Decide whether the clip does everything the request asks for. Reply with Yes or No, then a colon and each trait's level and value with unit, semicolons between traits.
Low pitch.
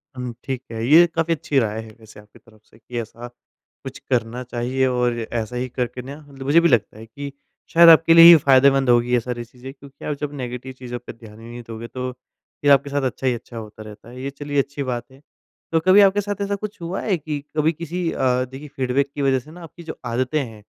Yes: low, 130 Hz